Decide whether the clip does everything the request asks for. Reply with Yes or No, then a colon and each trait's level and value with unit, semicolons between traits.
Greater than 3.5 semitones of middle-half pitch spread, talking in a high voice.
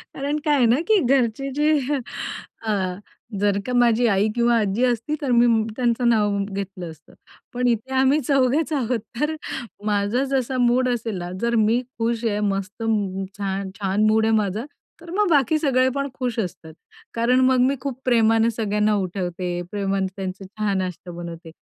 Yes: average, 4.2 semitones; high, 230 Hz